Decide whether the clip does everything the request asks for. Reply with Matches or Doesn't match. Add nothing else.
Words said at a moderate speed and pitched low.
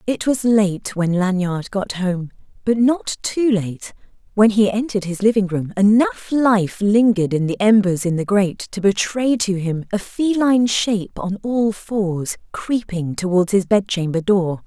Doesn't match